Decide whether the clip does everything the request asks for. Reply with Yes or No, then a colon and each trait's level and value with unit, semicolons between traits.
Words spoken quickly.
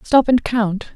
No: average, 190 wpm